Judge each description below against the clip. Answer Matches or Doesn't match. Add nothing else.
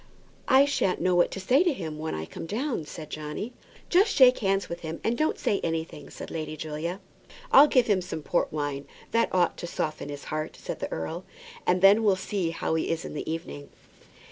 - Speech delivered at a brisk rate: Matches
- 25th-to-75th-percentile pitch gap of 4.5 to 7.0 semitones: Matches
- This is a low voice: Doesn't match